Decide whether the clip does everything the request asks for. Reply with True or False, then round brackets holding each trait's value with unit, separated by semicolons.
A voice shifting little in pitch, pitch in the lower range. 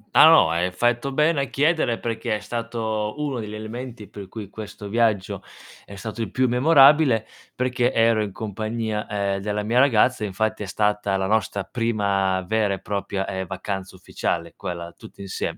False (3.1 semitones; 110 Hz)